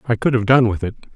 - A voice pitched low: Yes, low, 115 Hz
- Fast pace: Yes, fast, 310 wpm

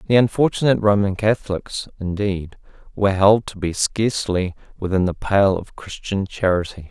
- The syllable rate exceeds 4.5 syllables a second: Yes, 5.1 syllables/s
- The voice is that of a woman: No, male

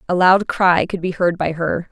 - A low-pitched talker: No, medium, 175 Hz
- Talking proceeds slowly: No, fast, 250 wpm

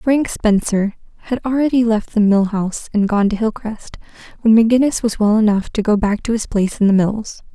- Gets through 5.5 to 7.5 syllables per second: Yes, 5.6 syllables/s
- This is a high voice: Yes, high, 215 Hz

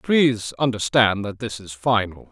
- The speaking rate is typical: Yes, average, 155 wpm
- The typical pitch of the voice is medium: No, low, 110 Hz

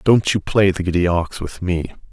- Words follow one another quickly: Yes, fast, 225 wpm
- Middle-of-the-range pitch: No, very low, 90 Hz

